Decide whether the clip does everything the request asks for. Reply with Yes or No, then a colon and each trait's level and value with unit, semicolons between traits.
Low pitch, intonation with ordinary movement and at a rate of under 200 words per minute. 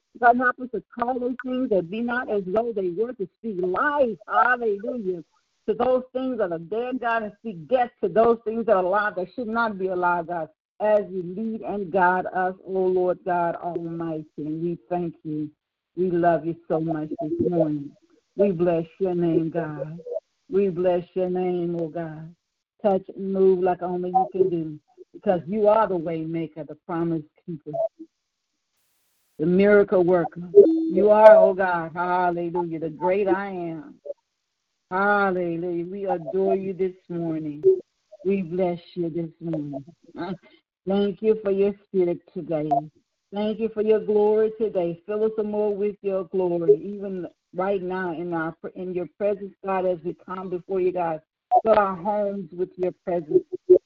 No: medium, 185 Hz; average, 3.6 semitones; average, 165 wpm